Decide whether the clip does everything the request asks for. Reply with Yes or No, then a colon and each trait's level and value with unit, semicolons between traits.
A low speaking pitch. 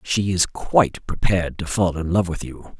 Yes: very low, 90 Hz